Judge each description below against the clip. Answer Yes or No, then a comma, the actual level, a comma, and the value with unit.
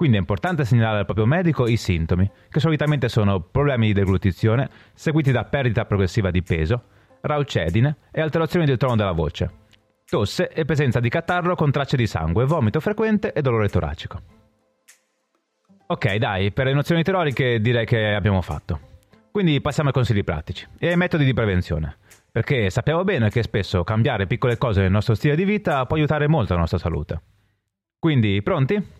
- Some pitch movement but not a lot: No, wide, 6.8 semitones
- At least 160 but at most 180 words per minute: Yes, fast, 170 wpm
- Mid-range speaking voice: No, low, 115 Hz